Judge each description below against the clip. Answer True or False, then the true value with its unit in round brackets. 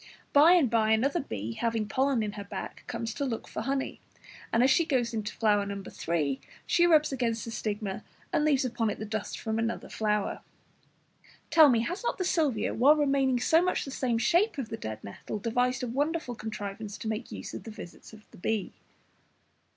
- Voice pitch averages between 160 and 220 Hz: False (230 Hz)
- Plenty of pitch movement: False (4.4 semitones)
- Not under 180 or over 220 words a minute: True (200 wpm)